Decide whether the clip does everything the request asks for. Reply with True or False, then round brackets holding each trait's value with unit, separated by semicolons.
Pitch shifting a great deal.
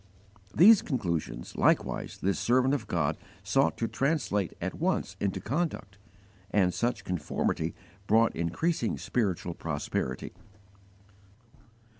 True (6.8 semitones)